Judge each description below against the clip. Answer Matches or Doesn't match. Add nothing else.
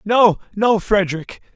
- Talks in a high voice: Matches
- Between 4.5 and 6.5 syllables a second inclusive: Doesn't match